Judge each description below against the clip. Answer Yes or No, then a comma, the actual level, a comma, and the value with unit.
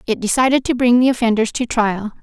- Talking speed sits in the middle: No, fast, 215 wpm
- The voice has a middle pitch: No, high, 235 Hz